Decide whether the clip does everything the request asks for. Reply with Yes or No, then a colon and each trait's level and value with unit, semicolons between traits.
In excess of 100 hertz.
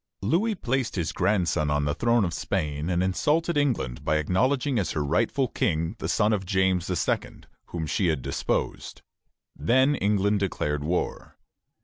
No: very low, 95 Hz